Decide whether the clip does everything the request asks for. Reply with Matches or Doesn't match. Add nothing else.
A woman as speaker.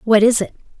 Matches